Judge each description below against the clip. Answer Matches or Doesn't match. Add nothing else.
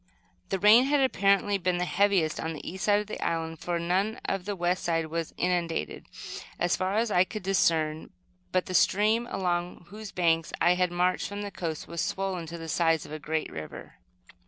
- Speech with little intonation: Doesn't match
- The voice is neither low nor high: Matches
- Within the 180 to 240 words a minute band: Matches